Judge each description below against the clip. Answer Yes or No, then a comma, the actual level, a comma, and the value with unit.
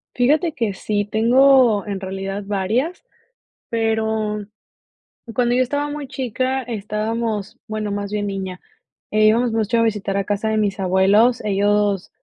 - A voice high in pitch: Yes, high, 215 Hz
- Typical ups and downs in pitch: Yes, average, 3.0 semitones